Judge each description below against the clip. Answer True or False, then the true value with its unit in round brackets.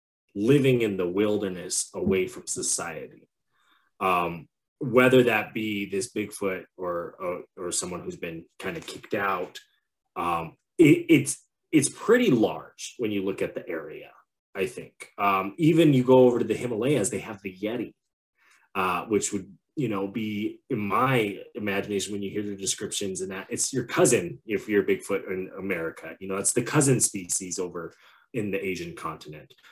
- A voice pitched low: True (100 Hz)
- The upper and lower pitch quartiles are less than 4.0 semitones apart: False (4.4 semitones)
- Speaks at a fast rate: False (170 wpm)